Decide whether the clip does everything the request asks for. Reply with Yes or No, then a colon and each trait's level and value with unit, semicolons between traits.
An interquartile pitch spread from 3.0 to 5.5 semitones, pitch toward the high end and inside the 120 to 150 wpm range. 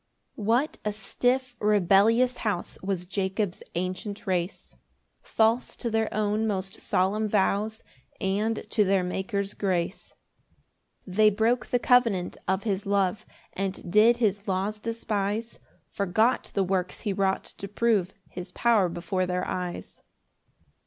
No: narrow, 2.6 semitones; high, 200 Hz; slow, 135 wpm